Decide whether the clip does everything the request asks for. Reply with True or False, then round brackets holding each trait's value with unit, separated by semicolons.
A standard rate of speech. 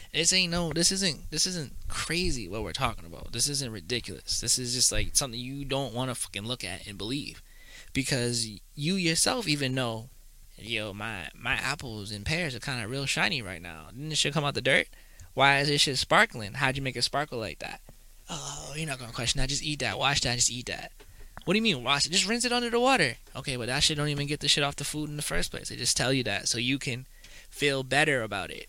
False (250 wpm)